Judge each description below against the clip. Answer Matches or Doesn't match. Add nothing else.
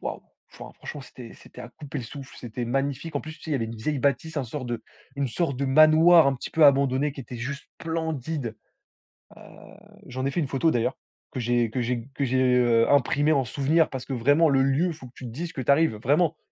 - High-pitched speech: Doesn't match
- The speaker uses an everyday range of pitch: Matches